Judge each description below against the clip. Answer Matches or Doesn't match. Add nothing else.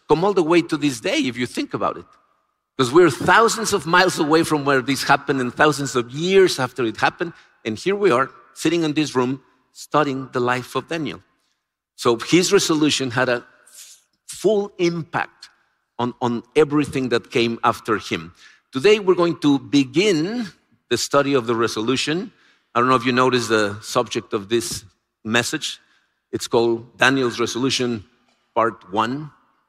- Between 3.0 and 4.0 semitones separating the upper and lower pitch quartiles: Doesn't match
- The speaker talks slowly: Doesn't match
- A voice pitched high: Doesn't match